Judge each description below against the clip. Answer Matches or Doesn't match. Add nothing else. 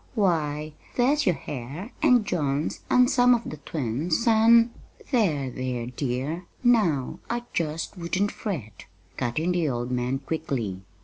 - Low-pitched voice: Doesn't match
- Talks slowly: Doesn't match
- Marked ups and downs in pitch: Matches